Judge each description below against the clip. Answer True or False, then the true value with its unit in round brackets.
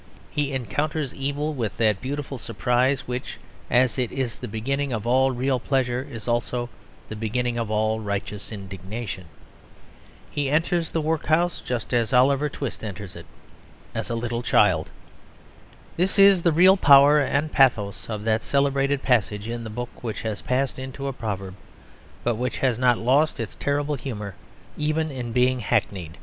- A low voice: True (125 Hz)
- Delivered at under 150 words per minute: False (160 wpm)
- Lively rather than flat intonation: False (3.9 semitones)